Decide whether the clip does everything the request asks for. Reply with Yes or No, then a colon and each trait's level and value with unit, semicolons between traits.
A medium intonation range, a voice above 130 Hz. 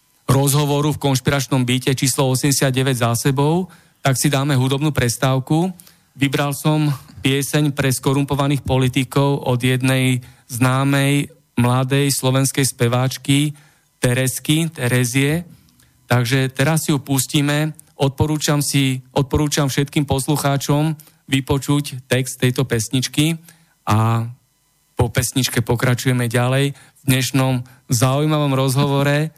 No: narrow, 2.1 semitones; medium, 140 Hz